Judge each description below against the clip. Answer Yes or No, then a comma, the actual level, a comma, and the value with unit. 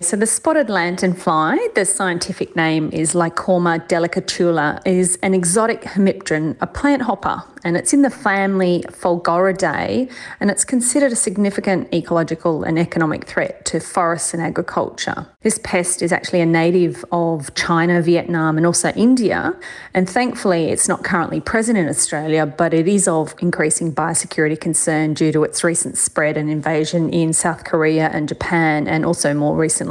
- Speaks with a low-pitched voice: No, medium, 175 Hz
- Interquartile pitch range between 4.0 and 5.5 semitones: No, average, 3.1 semitones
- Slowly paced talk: No, average, 160 wpm